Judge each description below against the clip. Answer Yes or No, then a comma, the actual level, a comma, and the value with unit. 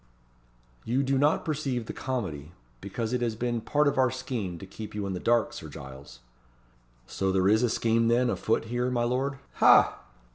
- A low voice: Yes, low, 120 Hz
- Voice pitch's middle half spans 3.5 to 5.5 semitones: Yes, average, 4.3 semitones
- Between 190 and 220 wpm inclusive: Yes, average, 195 wpm